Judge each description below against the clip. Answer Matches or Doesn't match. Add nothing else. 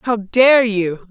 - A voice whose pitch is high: Matches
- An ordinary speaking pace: Matches